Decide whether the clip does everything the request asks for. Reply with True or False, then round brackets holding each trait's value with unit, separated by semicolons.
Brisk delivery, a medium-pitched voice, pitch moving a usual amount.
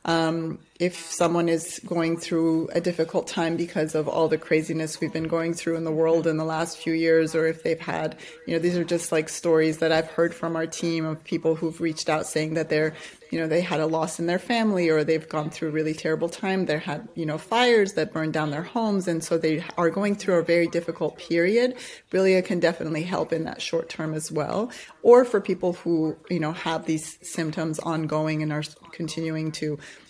False (225 wpm; 165 Hz; 1.3 semitones)